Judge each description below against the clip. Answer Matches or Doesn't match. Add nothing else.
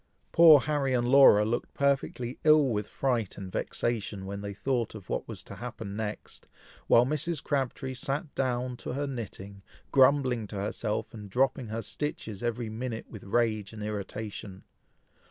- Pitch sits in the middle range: Doesn't match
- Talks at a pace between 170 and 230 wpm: Doesn't match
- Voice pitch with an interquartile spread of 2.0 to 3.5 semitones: Doesn't match